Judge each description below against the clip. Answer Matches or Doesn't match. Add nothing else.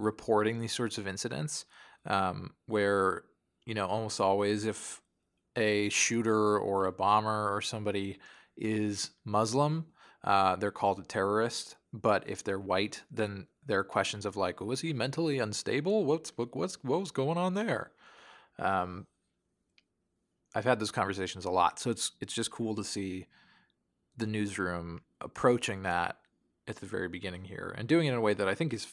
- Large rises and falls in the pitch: Doesn't match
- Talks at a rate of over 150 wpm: Matches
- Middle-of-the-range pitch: Doesn't match